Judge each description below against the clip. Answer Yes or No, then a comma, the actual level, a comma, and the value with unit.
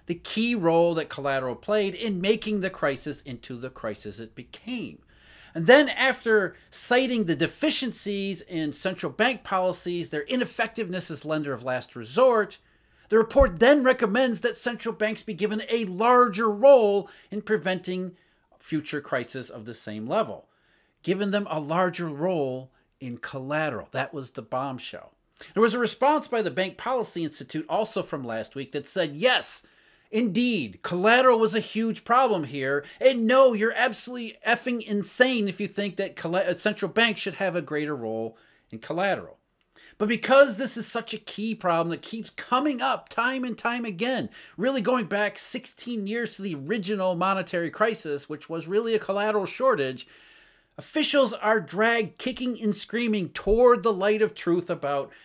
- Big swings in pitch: Yes, wide, 6.0 semitones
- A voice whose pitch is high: Yes, high, 210 Hz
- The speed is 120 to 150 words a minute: No, average, 160 wpm